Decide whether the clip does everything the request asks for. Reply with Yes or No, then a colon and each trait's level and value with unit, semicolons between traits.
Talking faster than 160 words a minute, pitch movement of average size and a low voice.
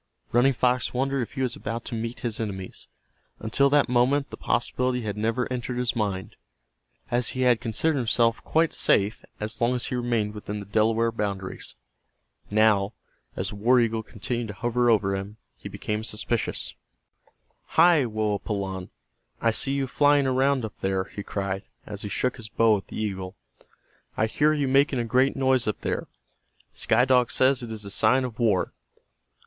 Yes: average, 175 wpm; average, 3.2 semitones; low, 115 Hz